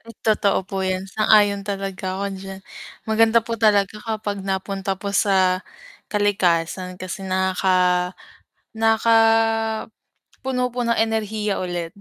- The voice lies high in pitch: Yes, high, 200 Hz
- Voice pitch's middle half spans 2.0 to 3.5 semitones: Yes, average, 2.7 semitones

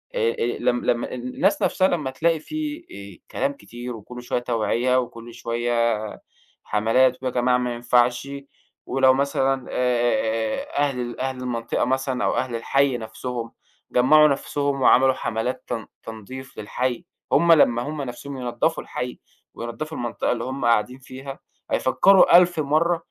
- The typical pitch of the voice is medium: No, low, 125 Hz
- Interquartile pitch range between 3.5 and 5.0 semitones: No, average, 2.7 semitones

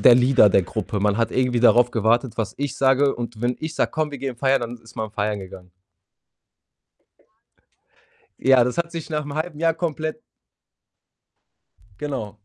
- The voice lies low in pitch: Yes, low, 125 Hz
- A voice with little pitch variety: No, average, 4.6 semitones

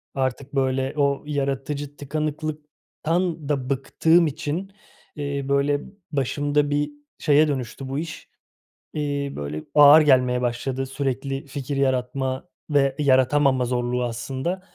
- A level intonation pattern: Yes, narrow, 2.0 semitones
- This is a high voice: No, medium, 140 Hz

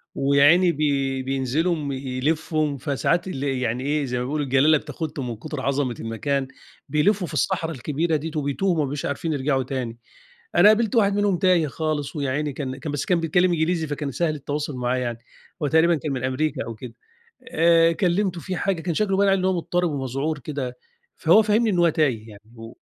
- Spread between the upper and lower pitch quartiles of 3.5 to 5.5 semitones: Yes, average, 4.1 semitones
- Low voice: No, medium, 150 Hz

